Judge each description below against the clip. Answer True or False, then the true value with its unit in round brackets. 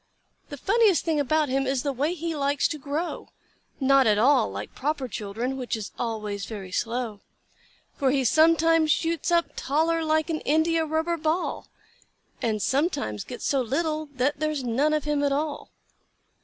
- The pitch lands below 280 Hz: False (285 Hz)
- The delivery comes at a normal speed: True (170 wpm)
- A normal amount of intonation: True (4.0 semitones)